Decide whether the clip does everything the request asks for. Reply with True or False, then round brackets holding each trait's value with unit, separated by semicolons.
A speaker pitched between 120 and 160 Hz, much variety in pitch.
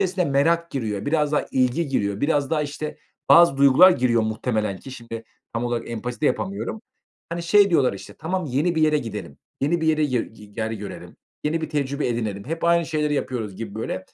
True (140 Hz; 5.9 semitones)